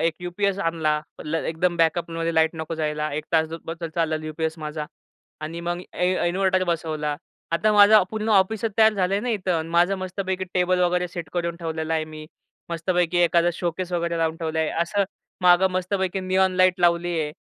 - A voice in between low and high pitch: Yes, medium, 175 Hz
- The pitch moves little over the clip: Yes, narrow, 2.3 semitones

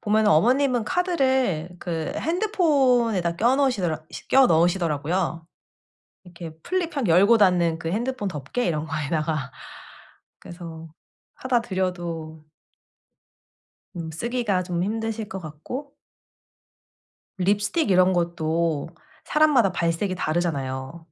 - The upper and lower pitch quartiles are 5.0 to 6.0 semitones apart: No, wide, 6.7 semitones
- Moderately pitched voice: Yes, medium, 180 Hz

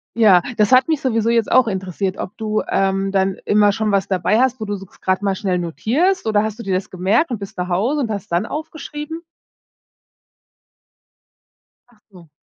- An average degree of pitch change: Yes, average, 3.7 semitones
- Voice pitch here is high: Yes, high, 210 Hz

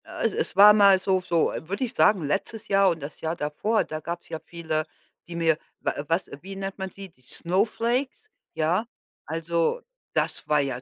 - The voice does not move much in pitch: No, average, 3.7 semitones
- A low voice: No, medium, 175 Hz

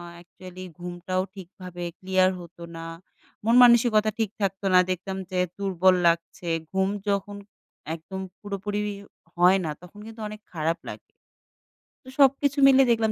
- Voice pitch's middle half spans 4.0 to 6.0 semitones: No, average, 2.8 semitones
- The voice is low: No, high, 190 Hz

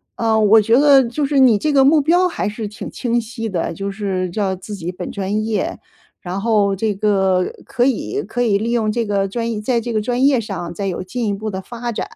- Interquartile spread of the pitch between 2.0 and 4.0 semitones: Yes, average, 3.5 semitones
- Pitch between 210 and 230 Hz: Yes, high, 215 Hz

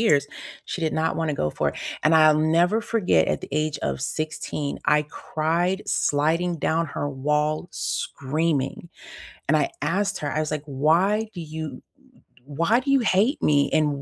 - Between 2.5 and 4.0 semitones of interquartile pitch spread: Yes, average, 2.9 semitones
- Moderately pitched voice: Yes, medium, 155 Hz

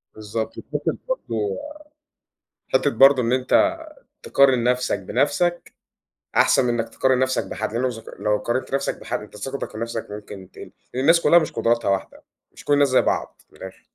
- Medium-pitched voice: No, low, 125 Hz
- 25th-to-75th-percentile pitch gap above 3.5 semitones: Yes, average, 3.9 semitones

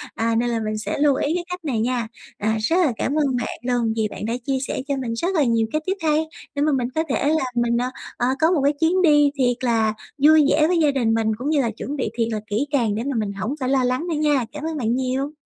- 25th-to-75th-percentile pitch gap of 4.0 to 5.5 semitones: Yes, average, 4.7 semitones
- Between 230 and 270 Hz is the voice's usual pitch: Yes, very high, 260 Hz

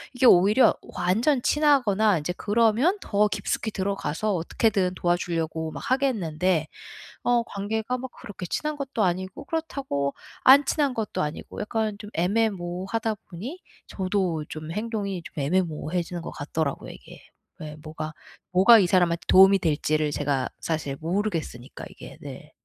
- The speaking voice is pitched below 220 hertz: Yes, high, 190 Hz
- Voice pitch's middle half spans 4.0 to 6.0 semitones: Yes, average, 5.2 semitones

